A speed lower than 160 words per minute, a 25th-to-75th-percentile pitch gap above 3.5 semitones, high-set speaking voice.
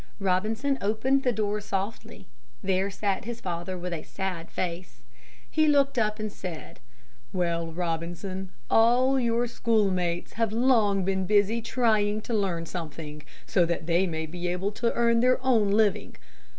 Yes: average, 150 wpm; average, 4.4 semitones; high, 200 Hz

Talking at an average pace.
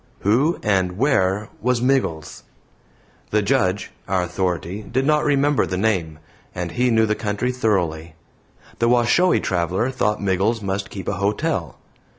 Yes: average, 145 wpm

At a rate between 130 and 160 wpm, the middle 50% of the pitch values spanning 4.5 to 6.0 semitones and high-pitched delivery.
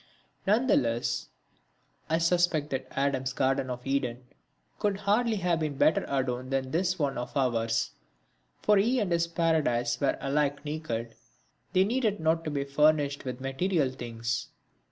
No: average, 155 wpm; average, 4.8 semitones; medium, 145 Hz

